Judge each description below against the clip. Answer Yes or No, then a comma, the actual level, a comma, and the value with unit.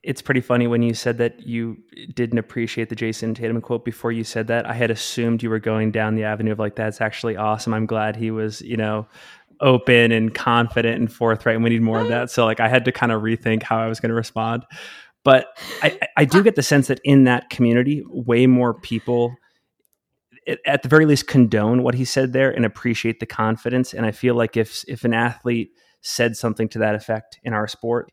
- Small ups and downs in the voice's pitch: Yes, narrow, 1.5 semitones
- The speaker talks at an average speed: No, fast, 230 wpm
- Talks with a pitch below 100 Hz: No, low, 115 Hz